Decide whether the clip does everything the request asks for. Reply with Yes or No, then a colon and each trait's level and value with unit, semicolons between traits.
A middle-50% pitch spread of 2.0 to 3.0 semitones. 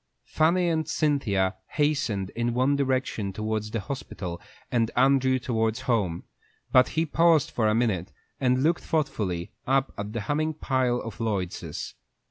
No: average, 4.9 semitones